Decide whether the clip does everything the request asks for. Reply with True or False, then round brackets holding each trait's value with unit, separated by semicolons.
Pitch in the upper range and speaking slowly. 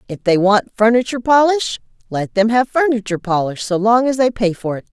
False (220 Hz; 205 wpm)